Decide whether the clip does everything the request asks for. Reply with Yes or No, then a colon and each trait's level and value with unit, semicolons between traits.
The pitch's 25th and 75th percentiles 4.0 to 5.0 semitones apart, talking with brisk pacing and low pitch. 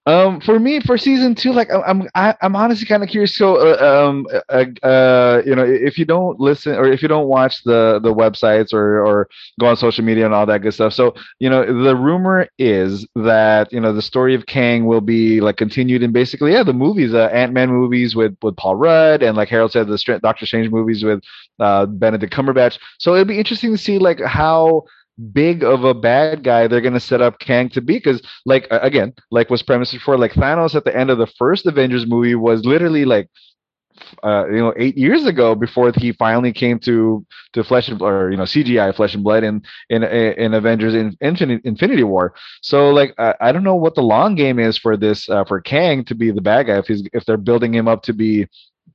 Yes: average, 4.3 semitones; fast, 230 wpm; low, 120 Hz